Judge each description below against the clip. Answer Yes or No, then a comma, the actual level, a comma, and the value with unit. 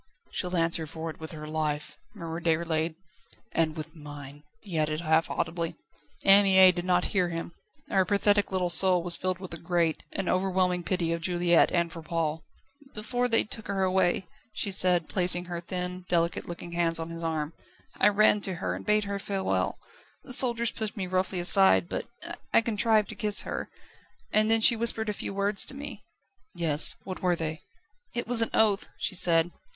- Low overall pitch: No, medium, 180 Hz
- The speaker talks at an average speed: Yes, average, 190 wpm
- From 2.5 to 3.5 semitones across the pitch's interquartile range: Yes, average, 3.2 semitones